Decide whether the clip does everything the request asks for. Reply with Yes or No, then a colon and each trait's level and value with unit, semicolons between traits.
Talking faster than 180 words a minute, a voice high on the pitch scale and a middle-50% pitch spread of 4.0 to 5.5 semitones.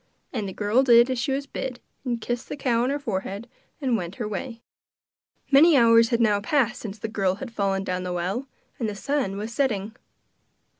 Yes: fast, 205 wpm; high, 230 Hz; average, 4.3 semitones